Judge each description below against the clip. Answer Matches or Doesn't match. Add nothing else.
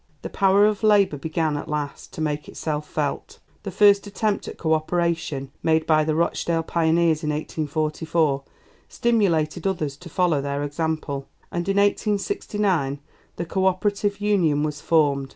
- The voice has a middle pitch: Matches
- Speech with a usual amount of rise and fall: Matches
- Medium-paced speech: Matches